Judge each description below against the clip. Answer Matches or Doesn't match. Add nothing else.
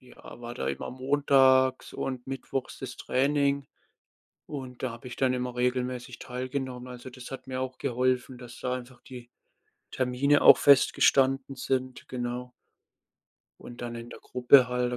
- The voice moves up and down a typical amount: Doesn't match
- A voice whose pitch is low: Matches